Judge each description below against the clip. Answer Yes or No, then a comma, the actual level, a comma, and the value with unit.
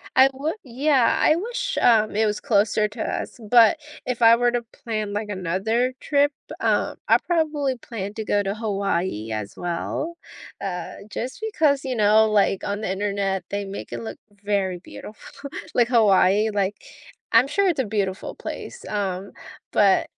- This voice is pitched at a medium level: No, high, 215 Hz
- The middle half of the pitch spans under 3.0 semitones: No, average, 4.5 semitones